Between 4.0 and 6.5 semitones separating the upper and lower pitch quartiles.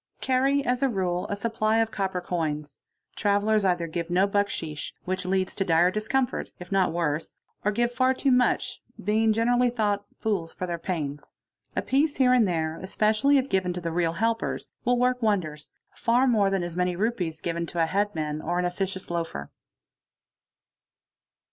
Yes: average, 4.9 semitones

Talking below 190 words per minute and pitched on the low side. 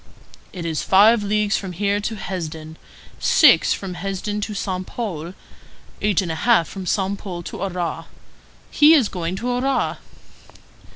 No: average, 155 wpm; high, 195 Hz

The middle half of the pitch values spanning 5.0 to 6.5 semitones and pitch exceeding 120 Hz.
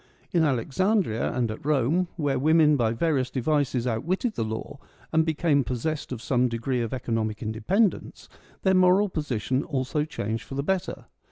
Yes: average, 5.3 semitones; medium, 140 Hz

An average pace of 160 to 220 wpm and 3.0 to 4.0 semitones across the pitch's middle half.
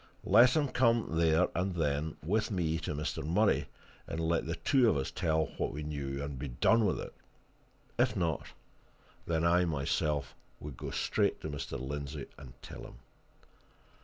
Yes: average, 170 wpm; average, 3.7 semitones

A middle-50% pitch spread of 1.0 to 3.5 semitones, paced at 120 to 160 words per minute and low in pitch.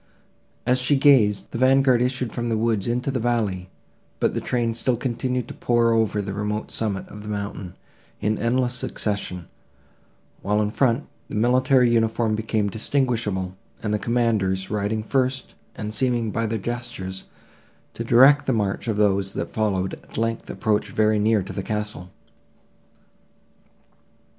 Yes: average, 2.8 semitones; average, 155 wpm; low, 110 Hz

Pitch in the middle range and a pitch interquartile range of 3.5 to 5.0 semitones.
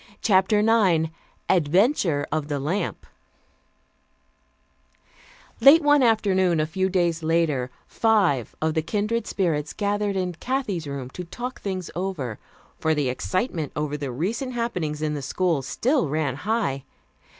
No: medium, 175 Hz; wide, 5.6 semitones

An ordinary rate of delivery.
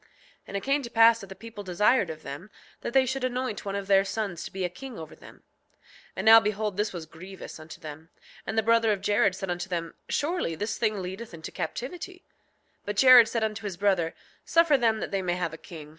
No: fast, 240 wpm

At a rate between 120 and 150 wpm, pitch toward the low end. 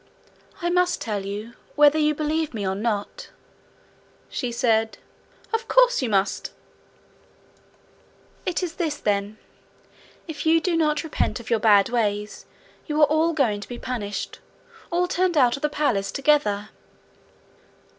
No: average, 145 wpm; very high, 275 Hz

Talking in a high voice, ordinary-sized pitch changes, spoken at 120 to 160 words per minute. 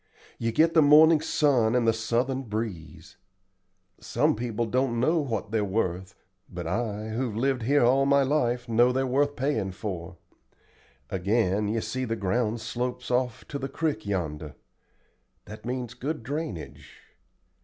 No: low, 120 Hz; average, 4.0 semitones; average, 150 wpm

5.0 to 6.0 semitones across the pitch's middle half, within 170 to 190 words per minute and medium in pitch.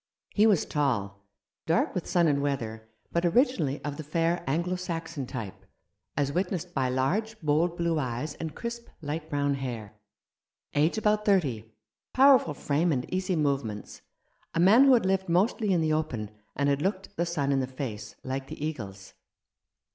Yes: average, 5.3 semitones; average, 185 wpm; medium, 155 Hz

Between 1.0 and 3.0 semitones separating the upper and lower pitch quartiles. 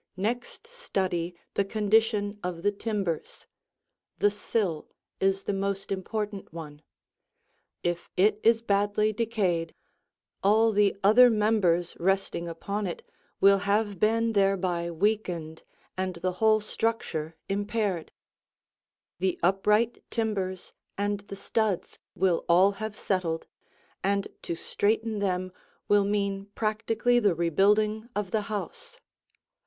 Yes: average, 2.7 semitones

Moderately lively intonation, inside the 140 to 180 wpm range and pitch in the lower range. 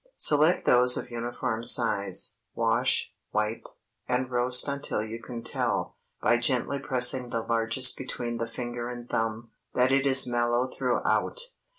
No: narrow, 1.6 semitones; average, 145 wpm; low, 120 Hz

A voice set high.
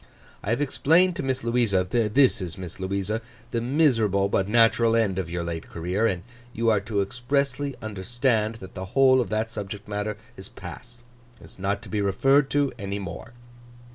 No: low, 110 Hz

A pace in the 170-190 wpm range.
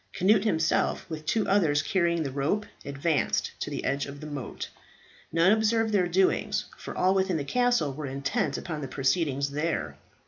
Yes: average, 175 wpm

